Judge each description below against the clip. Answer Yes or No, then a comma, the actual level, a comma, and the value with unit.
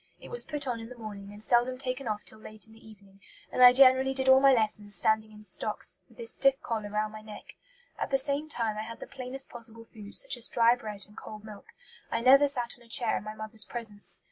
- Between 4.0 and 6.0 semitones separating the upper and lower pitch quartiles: No, average, 3.3 semitones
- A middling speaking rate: No, fast, 250 wpm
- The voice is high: Yes, high, 230 Hz